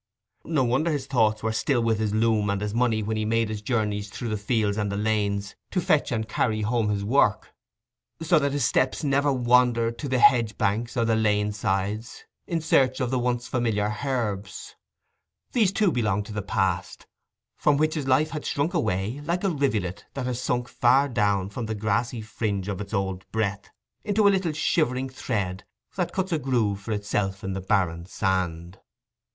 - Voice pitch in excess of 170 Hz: No, low, 110 Hz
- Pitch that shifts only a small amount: No, average, 4.3 semitones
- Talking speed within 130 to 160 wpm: No, average, 195 wpm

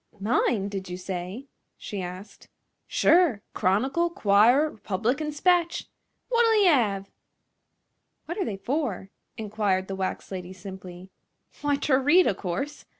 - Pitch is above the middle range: Yes, high, 215 Hz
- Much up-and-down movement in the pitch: Yes, wide, 7.6 semitones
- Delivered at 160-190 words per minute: No, slow, 135 wpm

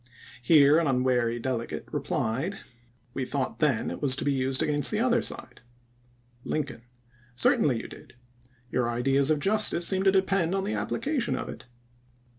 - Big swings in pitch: Yes, wide, 7.1 semitones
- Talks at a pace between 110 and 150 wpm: No, average, 165 wpm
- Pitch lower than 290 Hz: Yes, medium, 140 Hz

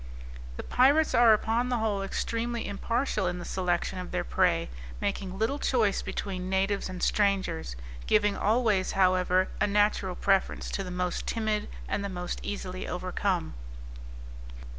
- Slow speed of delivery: No, average, 145 wpm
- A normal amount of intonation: Yes, average, 3.1 semitones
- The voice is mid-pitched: No, high, 195 Hz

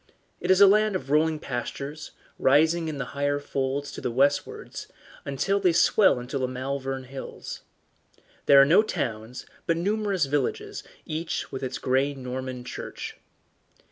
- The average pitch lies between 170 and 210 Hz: No, medium, 140 Hz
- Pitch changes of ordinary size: Yes, average, 3.9 semitones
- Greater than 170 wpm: No, average, 145 wpm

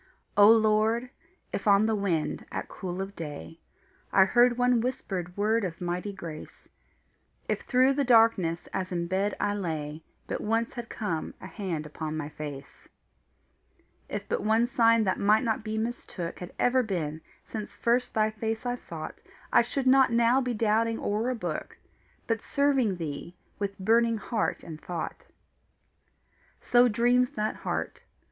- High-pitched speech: Yes, high, 215 Hz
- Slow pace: No, average, 160 wpm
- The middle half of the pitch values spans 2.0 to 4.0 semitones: No, average, 4.8 semitones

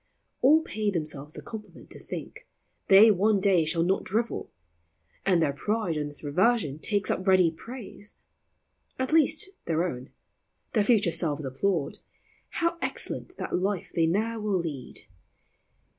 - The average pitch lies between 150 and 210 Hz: Yes, high, 190 Hz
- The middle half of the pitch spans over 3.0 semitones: Yes, average, 5.3 semitones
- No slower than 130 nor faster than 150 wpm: Yes, average, 145 wpm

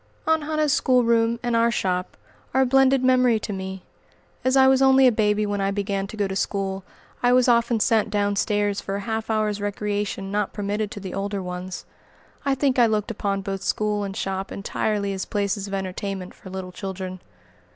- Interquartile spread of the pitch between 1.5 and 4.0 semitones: Yes, average, 3.2 semitones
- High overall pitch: Yes, high, 205 Hz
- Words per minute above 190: Yes, average, 200 wpm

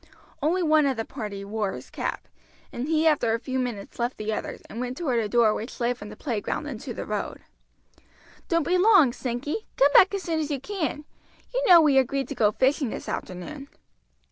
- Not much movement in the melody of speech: No, average, 5.3 semitones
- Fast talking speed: Yes, fast, 210 wpm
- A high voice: Yes, very high, 260 Hz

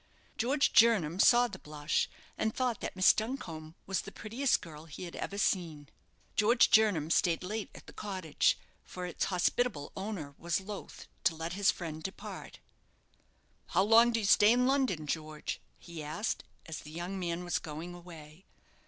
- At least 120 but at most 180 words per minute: Yes, average, 170 wpm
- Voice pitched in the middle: Yes, medium, 180 Hz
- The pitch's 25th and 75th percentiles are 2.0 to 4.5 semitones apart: No, average, 5.2 semitones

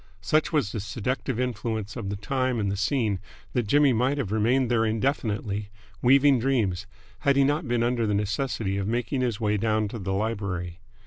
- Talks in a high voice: No, low, 115 Hz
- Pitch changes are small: No, average, 3.9 semitones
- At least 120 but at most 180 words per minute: No, average, 190 wpm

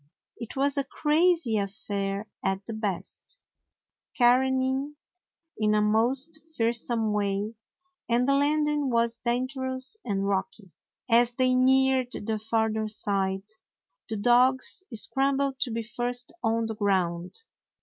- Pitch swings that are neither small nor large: Yes, average, 3.8 semitones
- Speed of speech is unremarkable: No, slow, 120 wpm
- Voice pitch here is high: Yes, high, 235 Hz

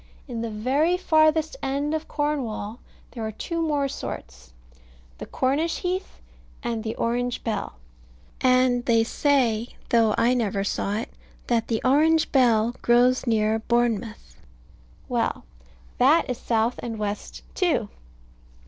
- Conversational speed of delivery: No, slow, 130 wpm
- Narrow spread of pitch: No, average, 4.4 semitones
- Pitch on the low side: No, high, 240 Hz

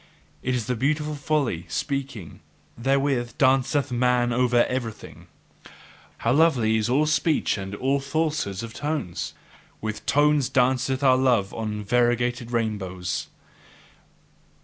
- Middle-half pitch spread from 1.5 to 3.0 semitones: No, average, 3.8 semitones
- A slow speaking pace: Yes, slow, 120 wpm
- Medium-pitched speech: No, low, 125 Hz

